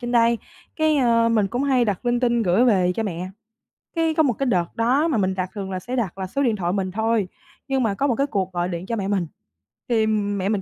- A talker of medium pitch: No, high, 220 Hz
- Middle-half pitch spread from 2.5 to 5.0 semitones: Yes, average, 4.3 semitones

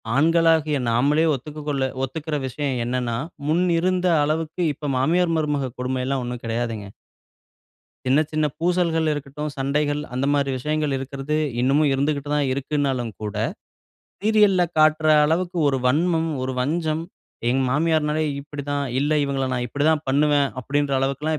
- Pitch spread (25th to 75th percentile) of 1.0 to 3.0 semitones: Yes, average, 2.7 semitones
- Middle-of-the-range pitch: Yes, medium, 145 Hz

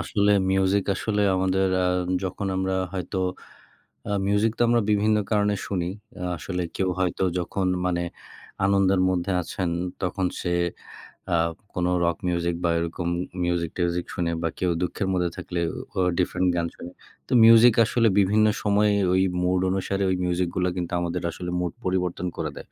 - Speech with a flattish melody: Yes, narrow, 2.1 semitones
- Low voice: Yes, very low, 95 Hz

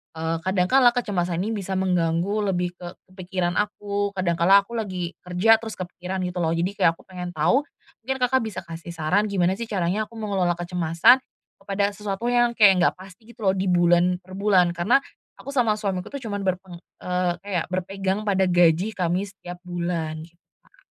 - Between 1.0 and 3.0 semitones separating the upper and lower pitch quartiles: Yes, average, 2.7 semitones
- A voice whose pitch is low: No, medium, 185 Hz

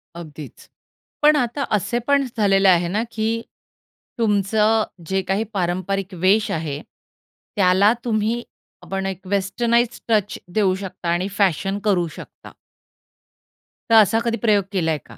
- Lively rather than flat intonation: No, average, 3.1 semitones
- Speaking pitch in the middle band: No, high, 200 Hz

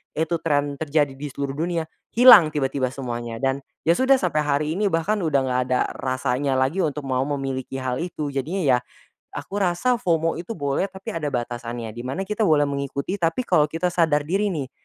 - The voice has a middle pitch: Yes, medium, 150 Hz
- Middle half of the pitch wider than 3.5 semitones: Yes, average, 4.5 semitones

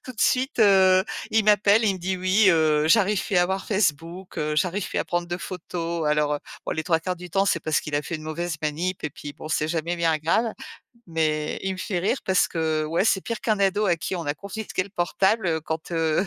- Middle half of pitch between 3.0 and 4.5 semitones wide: Yes, average, 3.4 semitones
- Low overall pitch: No, medium, 175 Hz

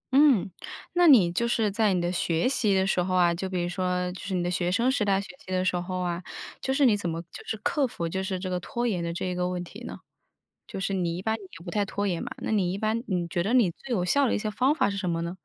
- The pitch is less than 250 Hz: Yes, high, 190 Hz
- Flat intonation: No, average, 3.5 semitones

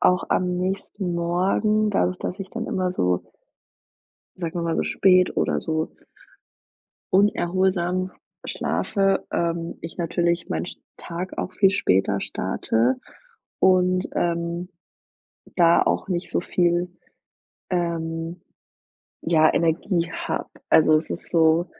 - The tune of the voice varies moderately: No, narrow, 1.8 semitones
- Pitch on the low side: No, medium, 175 Hz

